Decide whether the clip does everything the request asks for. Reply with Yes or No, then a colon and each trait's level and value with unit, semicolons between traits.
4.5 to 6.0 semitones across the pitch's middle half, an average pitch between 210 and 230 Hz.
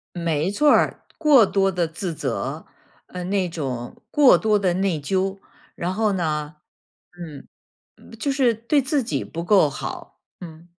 No: average, 5.0 semitones; medium, 185 Hz